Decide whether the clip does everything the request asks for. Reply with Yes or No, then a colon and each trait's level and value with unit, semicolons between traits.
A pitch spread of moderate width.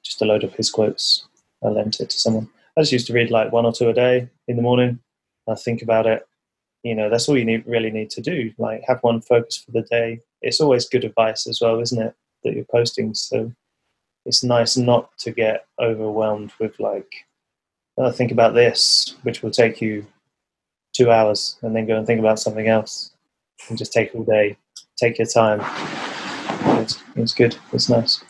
No: narrow, 1.4 semitones